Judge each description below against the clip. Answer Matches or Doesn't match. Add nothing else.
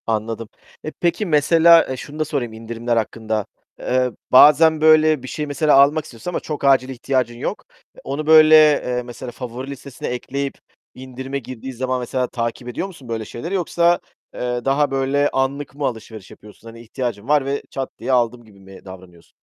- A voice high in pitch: Doesn't match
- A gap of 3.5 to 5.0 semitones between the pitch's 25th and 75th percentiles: Matches